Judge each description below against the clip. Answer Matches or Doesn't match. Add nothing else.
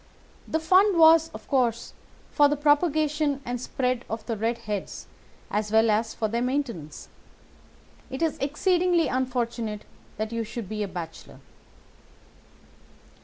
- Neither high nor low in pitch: Doesn't match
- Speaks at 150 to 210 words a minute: Doesn't match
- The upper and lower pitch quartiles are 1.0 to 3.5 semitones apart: Doesn't match